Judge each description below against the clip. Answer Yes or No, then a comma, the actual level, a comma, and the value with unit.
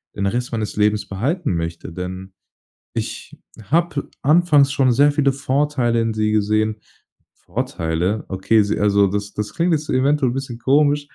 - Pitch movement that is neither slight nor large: No, wide, 5.7 semitones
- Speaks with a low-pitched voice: Yes, low, 115 Hz